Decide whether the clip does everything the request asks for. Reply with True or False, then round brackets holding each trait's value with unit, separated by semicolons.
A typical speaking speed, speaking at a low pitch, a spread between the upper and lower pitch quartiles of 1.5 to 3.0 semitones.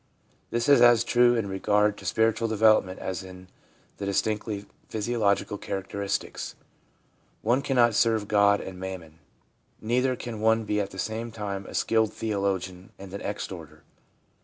True (150 wpm; 105 Hz; 2.7 semitones)